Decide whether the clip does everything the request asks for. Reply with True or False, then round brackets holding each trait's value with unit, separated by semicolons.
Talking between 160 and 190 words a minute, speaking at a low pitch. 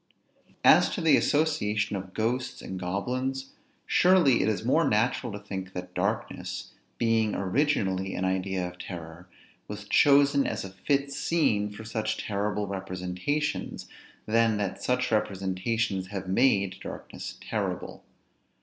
False (135 wpm; 105 Hz)